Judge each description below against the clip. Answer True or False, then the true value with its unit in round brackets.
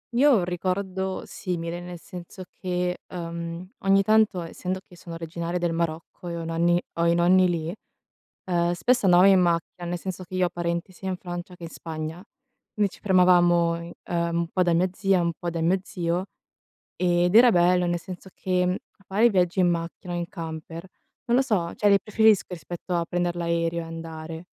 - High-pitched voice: False (175 Hz)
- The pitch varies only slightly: True (1.6 semitones)